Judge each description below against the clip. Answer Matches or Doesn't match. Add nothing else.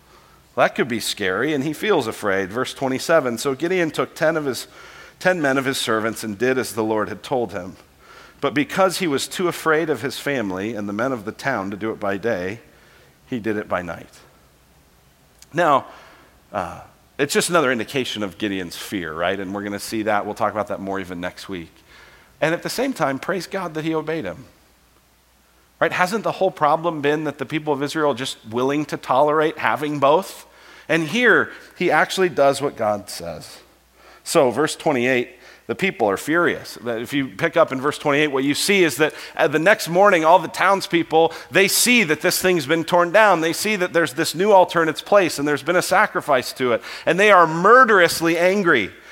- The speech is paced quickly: Matches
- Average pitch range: Doesn't match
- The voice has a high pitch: Doesn't match